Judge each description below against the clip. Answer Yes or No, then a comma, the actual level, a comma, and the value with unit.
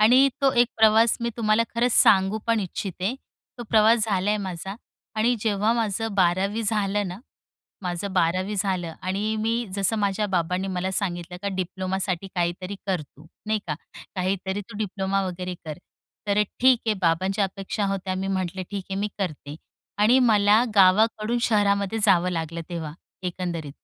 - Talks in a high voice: Yes, high, 195 Hz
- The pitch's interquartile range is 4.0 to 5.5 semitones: No, average, 2.7 semitones